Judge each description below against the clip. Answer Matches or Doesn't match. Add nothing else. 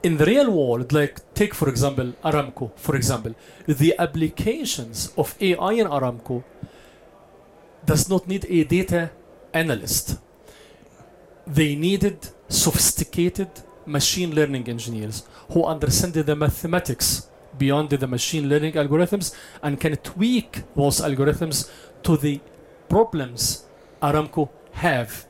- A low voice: Doesn't match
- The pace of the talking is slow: Matches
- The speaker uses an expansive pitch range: Doesn't match